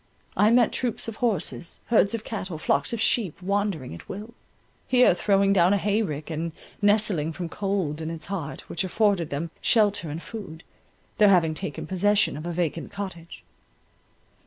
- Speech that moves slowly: No, average, 165 wpm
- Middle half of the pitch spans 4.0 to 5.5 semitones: Yes, average, 4.3 semitones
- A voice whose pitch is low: No, high, 190 Hz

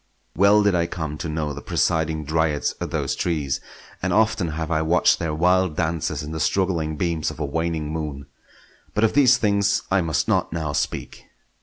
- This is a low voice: Yes, very low, 80 Hz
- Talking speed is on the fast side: No, average, 185 wpm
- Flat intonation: No, average, 3.0 semitones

